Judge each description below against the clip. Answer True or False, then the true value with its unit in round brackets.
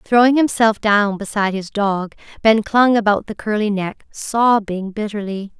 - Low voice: False (210 Hz)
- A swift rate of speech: False (150 wpm)